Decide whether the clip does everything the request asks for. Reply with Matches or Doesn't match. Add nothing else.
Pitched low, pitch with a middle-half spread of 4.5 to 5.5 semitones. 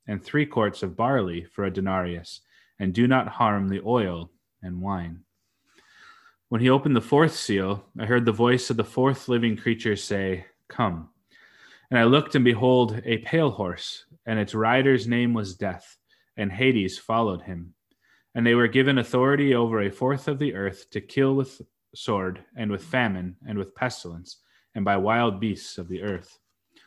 Matches